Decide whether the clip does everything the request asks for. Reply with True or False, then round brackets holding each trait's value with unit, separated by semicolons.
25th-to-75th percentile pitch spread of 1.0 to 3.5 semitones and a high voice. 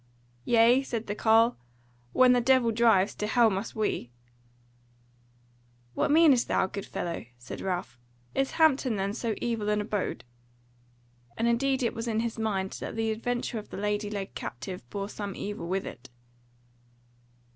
True (3.0 semitones; 220 Hz)